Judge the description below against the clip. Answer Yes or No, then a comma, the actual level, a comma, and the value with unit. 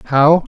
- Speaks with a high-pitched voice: No, medium, 150 Hz